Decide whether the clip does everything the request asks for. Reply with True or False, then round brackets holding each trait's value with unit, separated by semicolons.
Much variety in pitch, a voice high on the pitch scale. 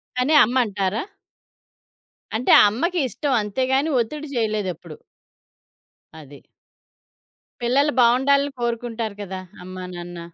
True (5.7 semitones; 235 Hz)